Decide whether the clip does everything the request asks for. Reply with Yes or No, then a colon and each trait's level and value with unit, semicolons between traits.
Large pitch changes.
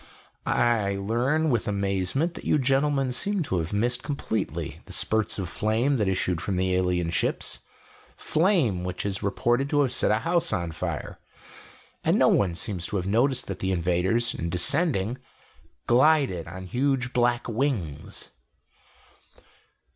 Yes: wide, 6.4 semitones